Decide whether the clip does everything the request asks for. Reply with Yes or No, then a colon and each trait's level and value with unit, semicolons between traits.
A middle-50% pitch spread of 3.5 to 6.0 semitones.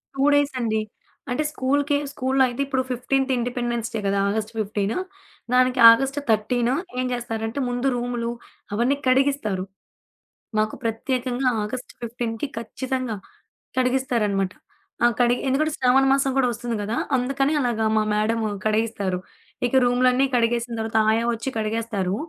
No: average, 2.8 semitones